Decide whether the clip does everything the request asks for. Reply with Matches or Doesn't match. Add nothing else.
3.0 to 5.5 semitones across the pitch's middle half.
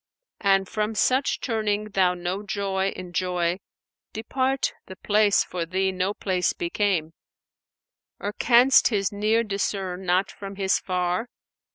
Doesn't match